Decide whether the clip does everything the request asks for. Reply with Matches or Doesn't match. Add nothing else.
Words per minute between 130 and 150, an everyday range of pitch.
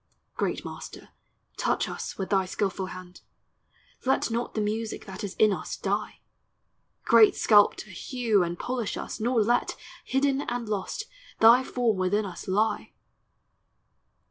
Matches